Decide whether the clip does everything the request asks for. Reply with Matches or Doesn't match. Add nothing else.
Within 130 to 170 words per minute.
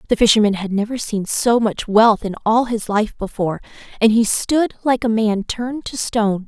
Doesn't match